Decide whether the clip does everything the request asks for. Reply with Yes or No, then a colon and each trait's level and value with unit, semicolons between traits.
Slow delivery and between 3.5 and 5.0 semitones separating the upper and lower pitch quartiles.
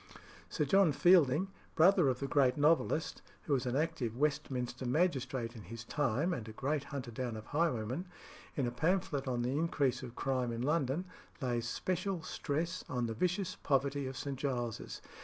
No: average, 175 wpm; average, 4.5 semitones